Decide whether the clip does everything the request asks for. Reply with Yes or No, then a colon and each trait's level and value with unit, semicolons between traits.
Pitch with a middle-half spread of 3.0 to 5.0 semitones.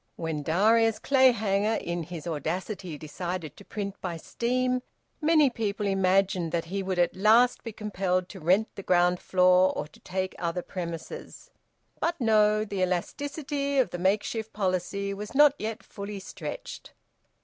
Yes: average, 3.8 semitones